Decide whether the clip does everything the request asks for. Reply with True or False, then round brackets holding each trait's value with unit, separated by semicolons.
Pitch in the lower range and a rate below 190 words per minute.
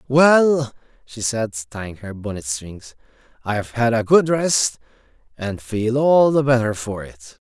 True (115 Hz; 155 wpm)